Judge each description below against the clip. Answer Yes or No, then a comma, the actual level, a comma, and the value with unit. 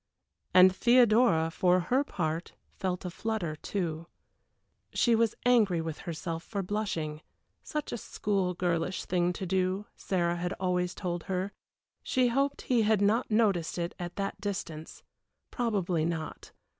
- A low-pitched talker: No, medium, 185 Hz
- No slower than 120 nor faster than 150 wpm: Yes, average, 145 wpm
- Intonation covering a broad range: No, average, 3.8 semitones